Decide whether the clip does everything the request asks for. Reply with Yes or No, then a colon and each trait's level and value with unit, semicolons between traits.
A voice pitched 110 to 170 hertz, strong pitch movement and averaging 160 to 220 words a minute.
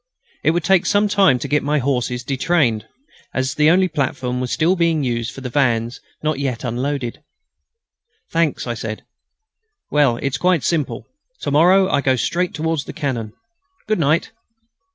No: medium, 140 Hz; average, 4.9 semitones; average, 165 wpm